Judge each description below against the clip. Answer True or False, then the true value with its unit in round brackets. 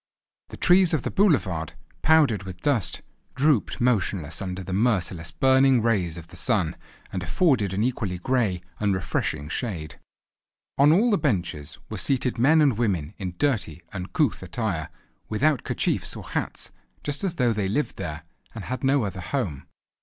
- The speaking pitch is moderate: False (105 Hz)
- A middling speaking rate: True (160 wpm)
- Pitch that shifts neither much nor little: False (7.1 semitones)